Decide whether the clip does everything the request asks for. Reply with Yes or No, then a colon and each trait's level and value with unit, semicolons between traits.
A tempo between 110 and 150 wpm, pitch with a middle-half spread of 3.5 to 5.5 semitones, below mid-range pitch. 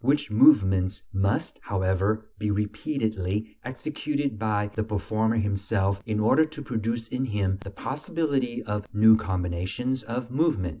Yes: slow, 135 wpm; average, 4.3 semitones; low, 110 Hz